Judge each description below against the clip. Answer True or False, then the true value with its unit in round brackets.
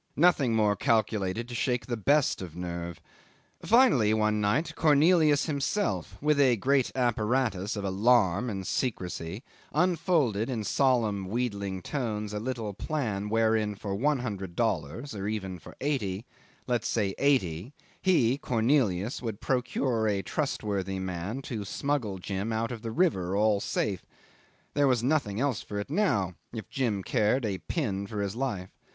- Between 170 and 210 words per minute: False (150 wpm)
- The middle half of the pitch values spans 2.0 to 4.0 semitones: False (5.1 semitones)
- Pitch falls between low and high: False (110 Hz)